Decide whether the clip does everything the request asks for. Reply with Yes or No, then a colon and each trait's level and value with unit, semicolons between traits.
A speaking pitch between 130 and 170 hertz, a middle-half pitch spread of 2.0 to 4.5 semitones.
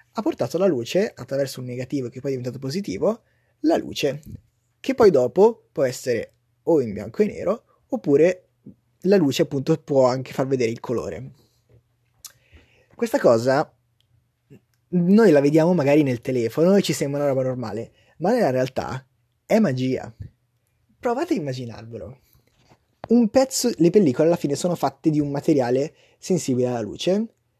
No: low, 135 Hz; wide, 5.6 semitones